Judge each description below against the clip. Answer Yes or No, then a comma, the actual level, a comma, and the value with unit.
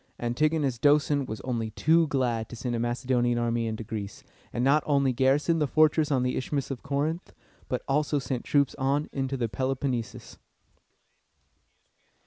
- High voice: No, low, 135 Hz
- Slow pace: No, average, 155 wpm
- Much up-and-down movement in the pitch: No, average, 3.3 semitones